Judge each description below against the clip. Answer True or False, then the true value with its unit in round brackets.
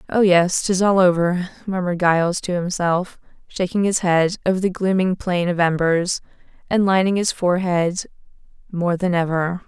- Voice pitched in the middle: True (180 Hz)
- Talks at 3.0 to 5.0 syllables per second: True (4.9 syllables/s)